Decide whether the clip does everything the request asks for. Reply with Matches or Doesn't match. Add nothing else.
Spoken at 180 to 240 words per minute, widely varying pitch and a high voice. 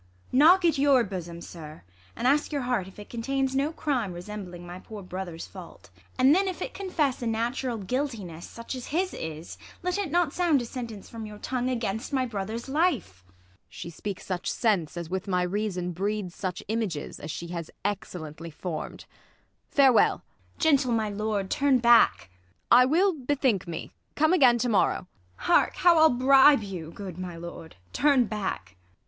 Matches